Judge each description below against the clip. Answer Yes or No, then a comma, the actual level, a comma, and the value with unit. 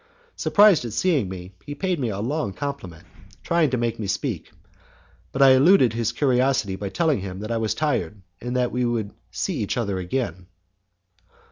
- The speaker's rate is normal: Yes, average, 180 wpm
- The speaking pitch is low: Yes, low, 120 Hz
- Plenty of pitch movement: Yes, wide, 5.7 semitones